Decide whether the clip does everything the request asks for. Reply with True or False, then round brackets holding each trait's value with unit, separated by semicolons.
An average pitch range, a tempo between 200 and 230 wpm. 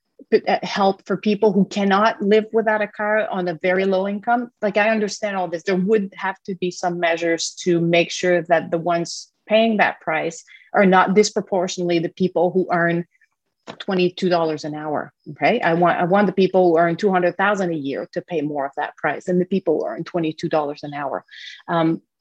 True (3.1 semitones; 205 wpm)